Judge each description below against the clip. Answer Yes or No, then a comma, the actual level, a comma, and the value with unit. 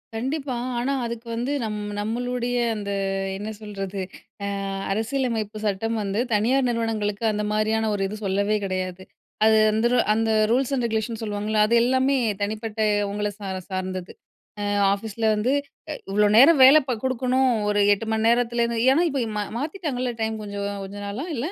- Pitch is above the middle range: Yes, high, 220 Hz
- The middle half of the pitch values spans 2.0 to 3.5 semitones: Yes, average, 3.1 semitones